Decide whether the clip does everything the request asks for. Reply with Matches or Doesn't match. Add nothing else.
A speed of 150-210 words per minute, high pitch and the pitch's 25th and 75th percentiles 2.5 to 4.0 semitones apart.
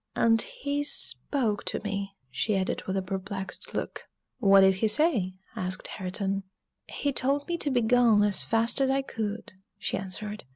Doesn't match